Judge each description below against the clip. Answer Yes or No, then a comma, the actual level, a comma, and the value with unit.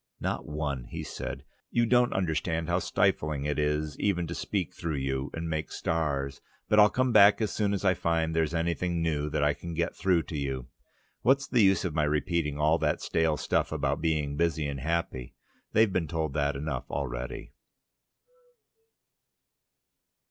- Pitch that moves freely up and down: No, average, 3.1 semitones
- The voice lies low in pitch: Yes, very low, 80 Hz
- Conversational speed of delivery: Yes, average, 175 wpm